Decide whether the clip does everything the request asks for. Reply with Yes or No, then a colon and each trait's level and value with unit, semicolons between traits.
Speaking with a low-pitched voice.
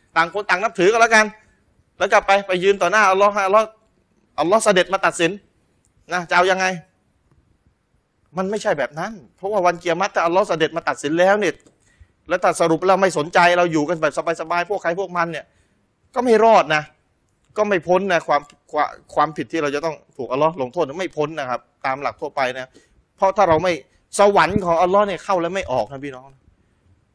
No: medium, 175 Hz